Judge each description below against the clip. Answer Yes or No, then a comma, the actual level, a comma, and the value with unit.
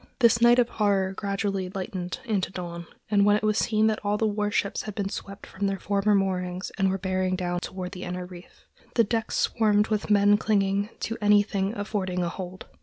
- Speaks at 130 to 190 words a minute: No, average, 200 wpm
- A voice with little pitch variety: Yes, narrow, 2.1 semitones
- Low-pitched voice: No, high, 200 Hz